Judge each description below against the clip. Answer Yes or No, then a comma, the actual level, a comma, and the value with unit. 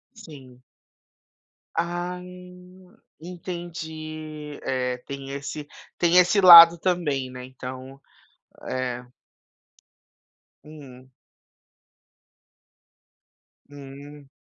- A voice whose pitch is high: No, medium, 155 Hz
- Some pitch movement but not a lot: Yes, average, 4.5 semitones